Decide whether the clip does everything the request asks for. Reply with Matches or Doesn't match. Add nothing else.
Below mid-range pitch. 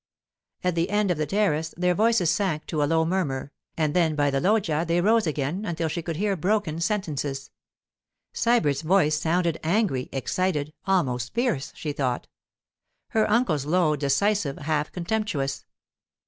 Doesn't match